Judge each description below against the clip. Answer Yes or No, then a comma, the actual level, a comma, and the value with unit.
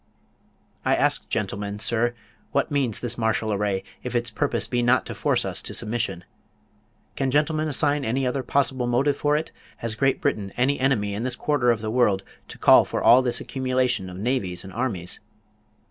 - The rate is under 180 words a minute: No, average, 185 wpm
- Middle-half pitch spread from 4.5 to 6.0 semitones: No, average, 3.8 semitones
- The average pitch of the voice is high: No, low, 120 Hz